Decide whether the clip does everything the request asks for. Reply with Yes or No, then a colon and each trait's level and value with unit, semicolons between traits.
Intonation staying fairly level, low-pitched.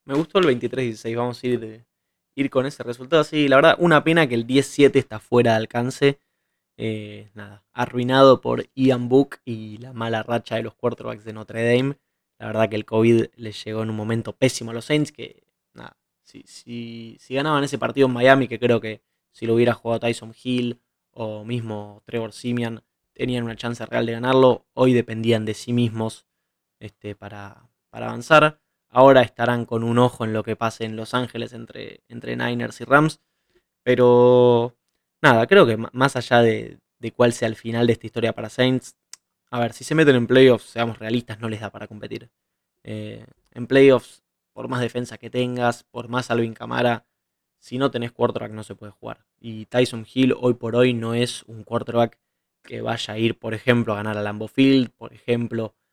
Yes: narrow, 2.1 semitones; low, 120 Hz